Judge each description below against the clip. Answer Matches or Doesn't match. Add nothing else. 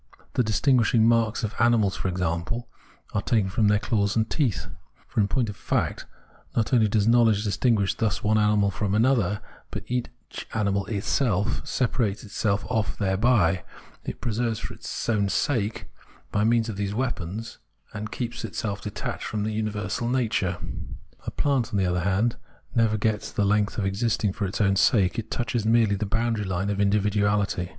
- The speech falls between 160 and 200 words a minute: Matches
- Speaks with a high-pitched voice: Doesn't match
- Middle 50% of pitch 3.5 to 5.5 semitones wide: Doesn't match